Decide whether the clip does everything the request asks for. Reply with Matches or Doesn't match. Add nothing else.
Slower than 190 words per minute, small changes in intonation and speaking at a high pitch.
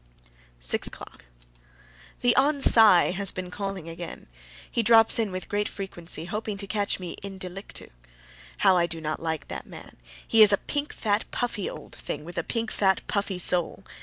Doesn't match